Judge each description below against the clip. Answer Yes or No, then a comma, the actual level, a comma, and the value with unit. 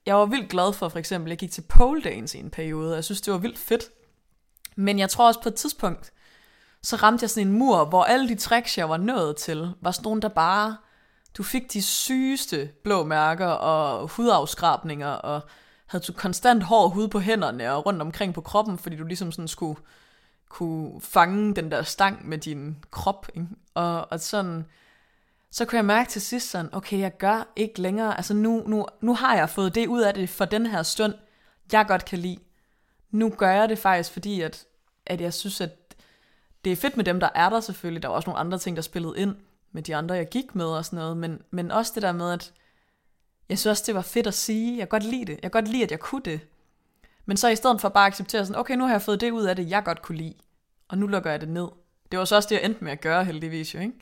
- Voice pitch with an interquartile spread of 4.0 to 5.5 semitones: Yes, average, 4.3 semitones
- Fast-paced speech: Yes, fast, 250 wpm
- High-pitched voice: Yes, high, 195 Hz